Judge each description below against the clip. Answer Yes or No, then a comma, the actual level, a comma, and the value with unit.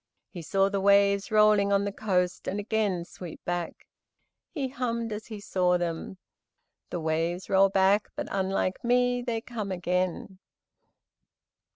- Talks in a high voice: Yes, high, 195 Hz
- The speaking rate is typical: Yes, average, 145 wpm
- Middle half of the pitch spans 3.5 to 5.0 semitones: No, average, 2.9 semitones